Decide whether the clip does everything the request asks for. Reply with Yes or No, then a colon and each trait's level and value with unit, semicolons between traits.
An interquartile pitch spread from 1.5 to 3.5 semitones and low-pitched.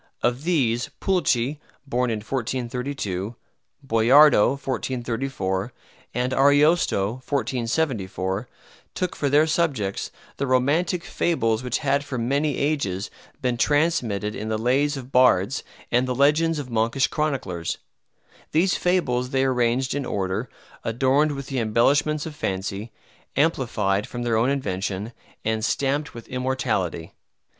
No: average, 4.1 semitones; low, 130 Hz